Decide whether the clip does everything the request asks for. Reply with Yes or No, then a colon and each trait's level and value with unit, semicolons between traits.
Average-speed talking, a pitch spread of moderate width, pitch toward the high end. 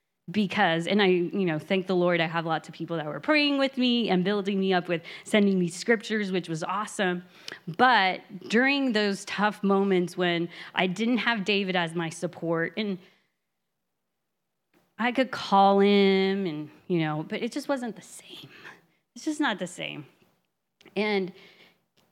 Yes: average, 170 wpm; average, 3.1 semitones; high, 195 Hz